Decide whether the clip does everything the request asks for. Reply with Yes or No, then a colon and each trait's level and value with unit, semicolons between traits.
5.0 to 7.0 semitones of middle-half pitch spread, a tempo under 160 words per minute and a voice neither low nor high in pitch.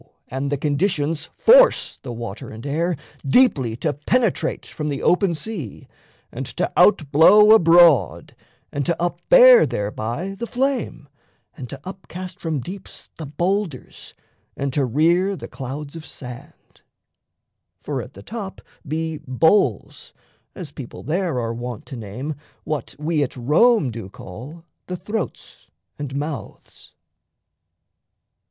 Yes: wide, 5.6 semitones; slow, 135 wpm; medium, 155 Hz